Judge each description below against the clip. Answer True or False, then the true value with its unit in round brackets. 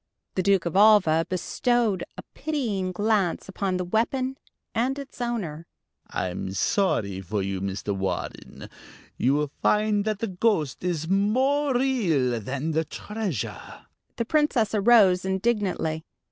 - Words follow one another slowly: True (130 wpm)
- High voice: True (195 Hz)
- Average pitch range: False (6.4 semitones)